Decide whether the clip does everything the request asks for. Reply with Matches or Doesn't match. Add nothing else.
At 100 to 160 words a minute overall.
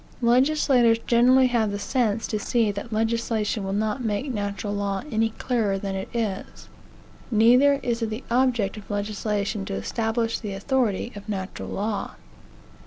Matches